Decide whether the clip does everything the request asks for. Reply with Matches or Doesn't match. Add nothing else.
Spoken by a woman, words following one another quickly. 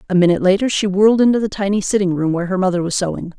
Matches